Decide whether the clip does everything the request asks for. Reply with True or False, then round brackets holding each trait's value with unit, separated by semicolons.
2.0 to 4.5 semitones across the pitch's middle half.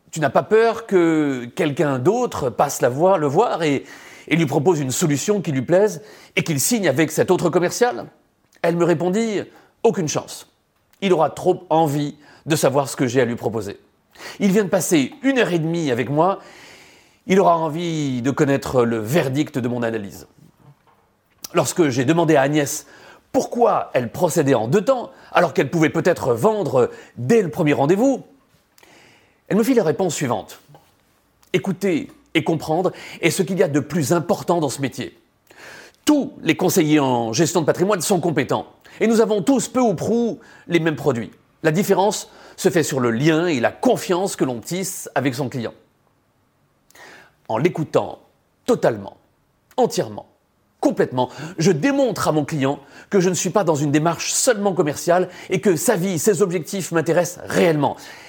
False (5.0 semitones)